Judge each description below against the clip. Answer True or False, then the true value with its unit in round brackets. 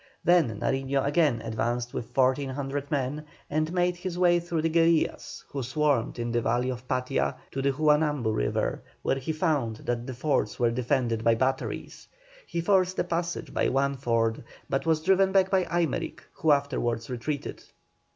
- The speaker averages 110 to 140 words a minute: False (170 wpm)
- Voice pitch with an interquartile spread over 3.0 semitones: True (5.0 semitones)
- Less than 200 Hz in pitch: True (140 Hz)